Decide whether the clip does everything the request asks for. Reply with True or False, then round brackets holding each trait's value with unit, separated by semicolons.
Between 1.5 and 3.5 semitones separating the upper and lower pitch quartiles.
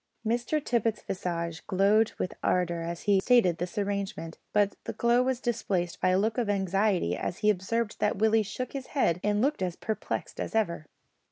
False (4.0 semitones)